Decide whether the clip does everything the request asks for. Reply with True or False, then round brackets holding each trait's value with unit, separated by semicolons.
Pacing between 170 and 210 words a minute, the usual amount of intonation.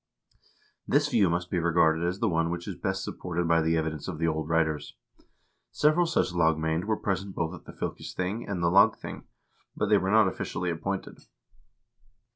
True (180 wpm; 3.0 semitones)